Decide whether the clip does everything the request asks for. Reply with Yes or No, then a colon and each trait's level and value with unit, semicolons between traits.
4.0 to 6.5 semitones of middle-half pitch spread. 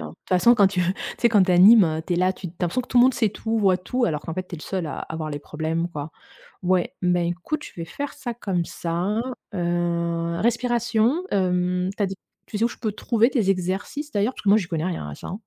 Yes: average, 4.5 semitones